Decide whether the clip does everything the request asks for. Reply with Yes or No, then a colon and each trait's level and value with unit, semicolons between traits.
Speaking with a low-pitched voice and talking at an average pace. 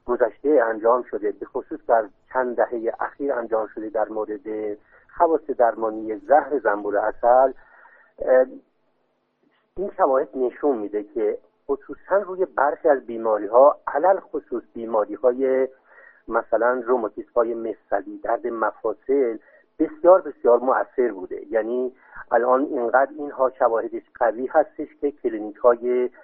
Yes: low, 130 Hz; average, 120 wpm